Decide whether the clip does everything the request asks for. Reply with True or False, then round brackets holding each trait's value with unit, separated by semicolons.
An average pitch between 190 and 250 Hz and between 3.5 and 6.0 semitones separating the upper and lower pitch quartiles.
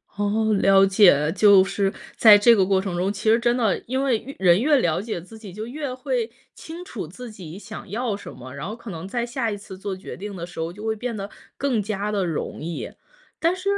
True (210 Hz; 3.8 semitones)